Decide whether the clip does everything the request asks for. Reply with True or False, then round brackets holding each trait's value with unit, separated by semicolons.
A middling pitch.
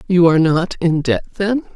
True (180 Hz)